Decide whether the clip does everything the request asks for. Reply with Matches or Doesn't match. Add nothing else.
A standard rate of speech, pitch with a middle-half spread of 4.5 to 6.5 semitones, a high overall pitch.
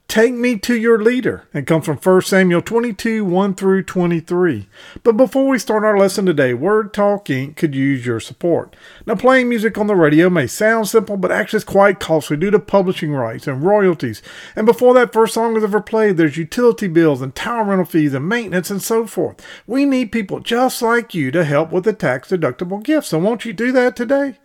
Doesn't match